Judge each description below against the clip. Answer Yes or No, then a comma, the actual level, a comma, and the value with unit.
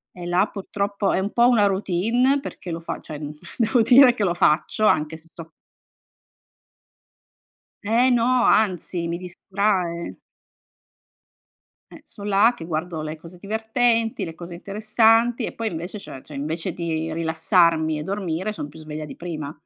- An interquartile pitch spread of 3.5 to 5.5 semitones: Yes, average, 5.1 semitones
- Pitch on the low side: No, medium, 185 Hz